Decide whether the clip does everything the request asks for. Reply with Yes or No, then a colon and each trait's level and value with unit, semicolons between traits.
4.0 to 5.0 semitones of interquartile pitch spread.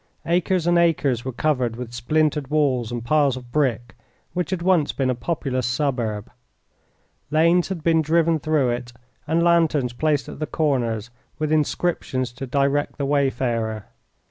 Yes: average, 4.3 semitones